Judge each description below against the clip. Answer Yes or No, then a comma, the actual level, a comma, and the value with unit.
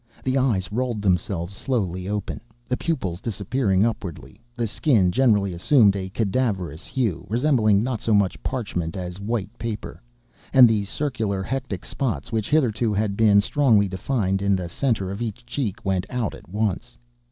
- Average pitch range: Yes, average, 4.1 semitones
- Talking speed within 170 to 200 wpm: No, average, 160 wpm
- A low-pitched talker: Yes, low, 105 Hz